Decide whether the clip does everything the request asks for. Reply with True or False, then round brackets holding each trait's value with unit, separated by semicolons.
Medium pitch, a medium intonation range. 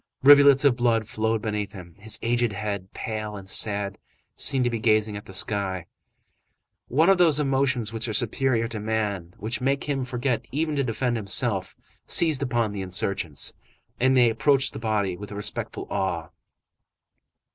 False (110 Hz; 4.2 semitones)